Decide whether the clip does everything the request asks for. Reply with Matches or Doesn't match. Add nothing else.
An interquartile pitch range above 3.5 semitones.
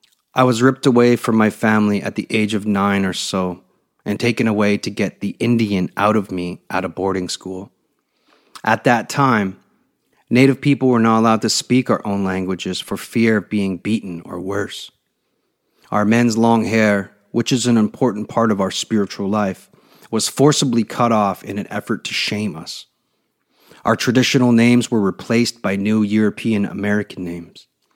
Doesn't match